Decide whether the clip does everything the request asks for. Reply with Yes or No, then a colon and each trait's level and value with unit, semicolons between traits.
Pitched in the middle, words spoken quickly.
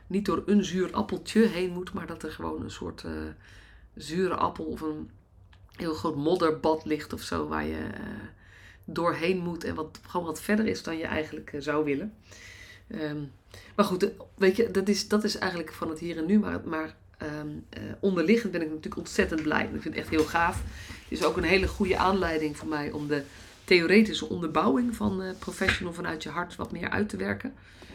Yes: medium, 160 Hz; fast, 210 wpm